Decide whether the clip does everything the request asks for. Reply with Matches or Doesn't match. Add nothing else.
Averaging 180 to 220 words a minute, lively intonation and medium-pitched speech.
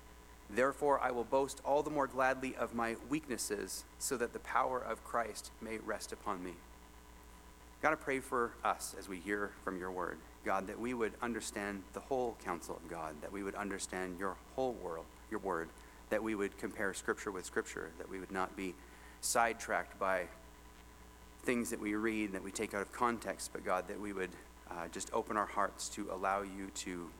Doesn't match